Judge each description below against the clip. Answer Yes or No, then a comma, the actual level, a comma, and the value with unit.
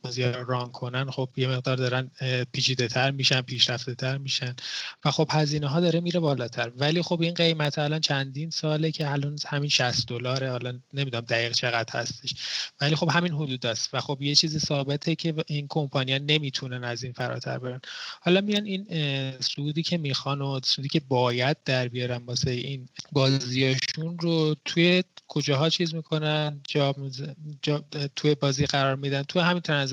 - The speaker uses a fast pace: Yes, fast, 165 wpm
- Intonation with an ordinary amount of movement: Yes, average, 3.1 semitones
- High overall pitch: No, medium, 140 Hz